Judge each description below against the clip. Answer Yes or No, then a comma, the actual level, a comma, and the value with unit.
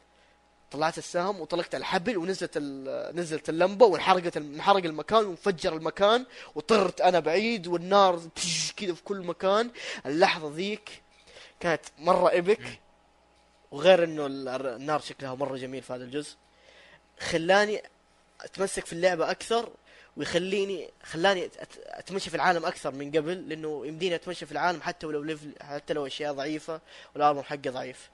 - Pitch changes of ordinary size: Yes, average, 4.0 semitones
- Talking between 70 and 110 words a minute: No, average, 130 wpm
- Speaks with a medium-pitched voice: Yes, medium, 170 Hz